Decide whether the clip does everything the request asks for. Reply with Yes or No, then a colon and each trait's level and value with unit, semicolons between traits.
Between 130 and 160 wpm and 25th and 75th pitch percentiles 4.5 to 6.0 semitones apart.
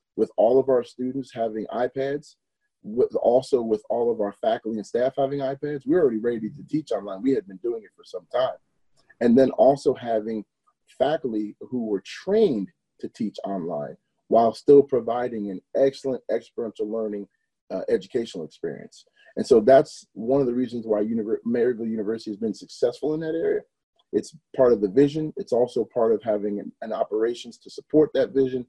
No: average, 185 wpm; wide, 5.5 semitones